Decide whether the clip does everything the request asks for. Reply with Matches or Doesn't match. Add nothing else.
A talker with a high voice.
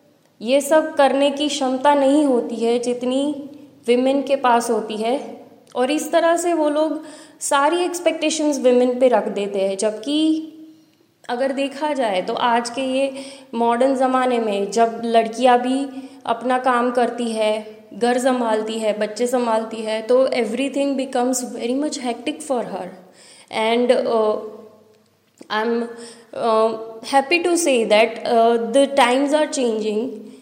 Matches